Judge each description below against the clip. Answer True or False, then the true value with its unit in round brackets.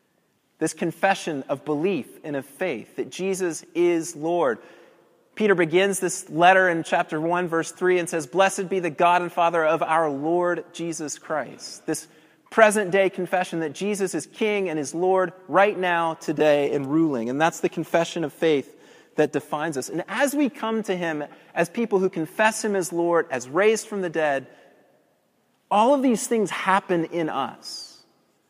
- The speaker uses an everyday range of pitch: True (3.1 semitones)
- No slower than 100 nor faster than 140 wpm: False (175 wpm)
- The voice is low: False (175 Hz)